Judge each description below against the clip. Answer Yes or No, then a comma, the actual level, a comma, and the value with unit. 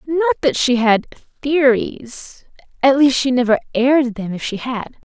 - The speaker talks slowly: No, average, 150 wpm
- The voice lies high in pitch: Yes, very high, 260 Hz